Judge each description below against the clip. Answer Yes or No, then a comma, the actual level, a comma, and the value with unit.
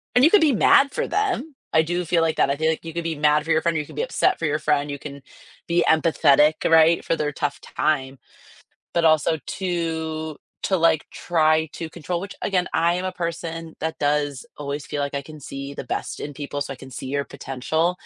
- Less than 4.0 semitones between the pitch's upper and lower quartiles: Yes, narrow, 2.6 semitones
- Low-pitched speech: No, medium, 160 Hz